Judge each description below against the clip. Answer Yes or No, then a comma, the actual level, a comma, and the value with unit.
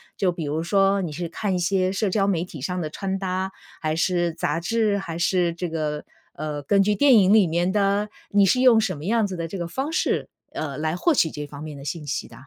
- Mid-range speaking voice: Yes, medium, 180 Hz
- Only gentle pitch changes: No, average, 3.7 semitones